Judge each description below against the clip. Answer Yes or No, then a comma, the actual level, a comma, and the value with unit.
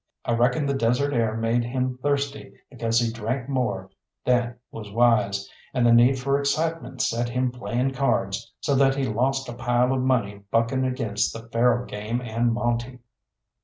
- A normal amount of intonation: No, narrow, 2.3 semitones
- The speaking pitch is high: No, low, 120 Hz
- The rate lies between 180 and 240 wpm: No, average, 170 wpm